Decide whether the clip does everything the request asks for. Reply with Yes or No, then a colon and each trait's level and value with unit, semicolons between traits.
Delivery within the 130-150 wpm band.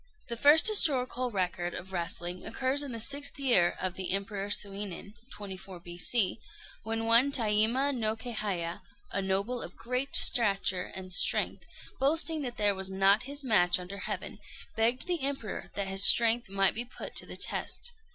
No: average, 165 wpm